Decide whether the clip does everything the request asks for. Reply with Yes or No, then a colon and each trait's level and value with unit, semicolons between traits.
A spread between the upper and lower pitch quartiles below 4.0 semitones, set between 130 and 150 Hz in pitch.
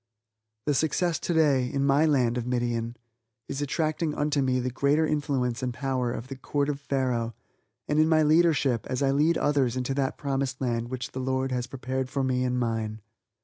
Yes: average, 2.7 semitones; low, 135 Hz